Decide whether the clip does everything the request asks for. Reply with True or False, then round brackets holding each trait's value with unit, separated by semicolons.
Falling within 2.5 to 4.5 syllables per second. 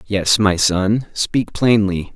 True (3.1 syllables/s)